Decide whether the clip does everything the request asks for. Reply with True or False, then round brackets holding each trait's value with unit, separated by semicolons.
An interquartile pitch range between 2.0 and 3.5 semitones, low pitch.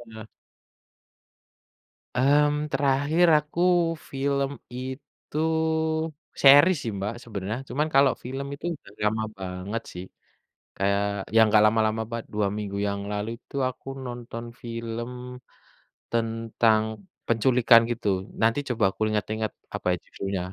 False (4.1 semitones; 115 Hz)